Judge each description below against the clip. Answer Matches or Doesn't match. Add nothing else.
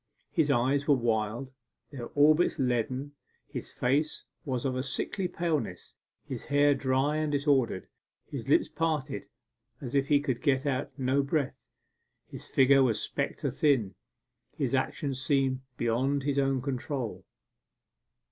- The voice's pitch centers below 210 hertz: Matches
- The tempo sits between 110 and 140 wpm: Matches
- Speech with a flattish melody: Matches